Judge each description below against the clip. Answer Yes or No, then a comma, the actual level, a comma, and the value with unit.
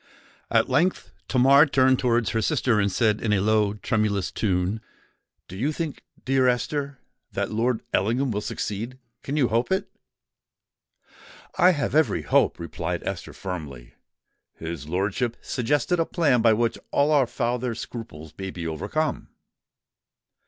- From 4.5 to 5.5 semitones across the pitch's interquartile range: Yes, average, 5.0 semitones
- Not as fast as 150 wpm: Yes, average, 140 wpm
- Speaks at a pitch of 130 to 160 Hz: No, low, 115 Hz